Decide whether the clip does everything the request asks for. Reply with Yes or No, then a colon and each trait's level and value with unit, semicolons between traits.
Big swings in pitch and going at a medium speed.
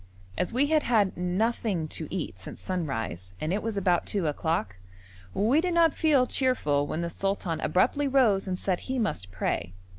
Yes: wide, 7.7 semitones; average, 180 wpm